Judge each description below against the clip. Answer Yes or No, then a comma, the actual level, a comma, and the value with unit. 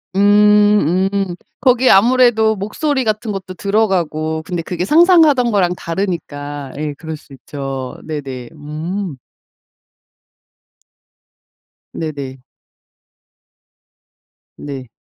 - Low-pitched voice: No, medium, 185 Hz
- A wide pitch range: Yes, wide, 6.0 semitones